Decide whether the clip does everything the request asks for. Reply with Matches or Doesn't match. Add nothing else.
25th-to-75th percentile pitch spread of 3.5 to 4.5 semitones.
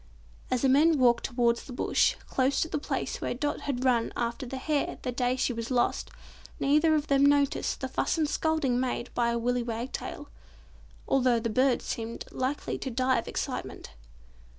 Doesn't match